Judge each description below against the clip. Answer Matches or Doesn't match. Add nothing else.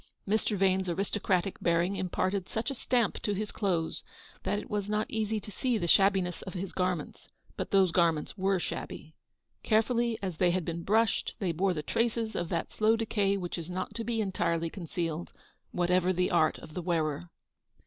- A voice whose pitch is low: Doesn't match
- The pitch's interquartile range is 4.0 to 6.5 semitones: Doesn't match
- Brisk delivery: Doesn't match